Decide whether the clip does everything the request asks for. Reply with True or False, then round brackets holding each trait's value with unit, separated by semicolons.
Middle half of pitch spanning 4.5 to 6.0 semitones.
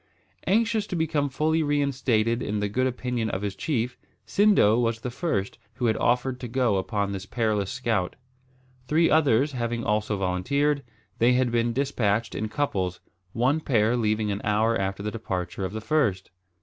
True (4.9 semitones)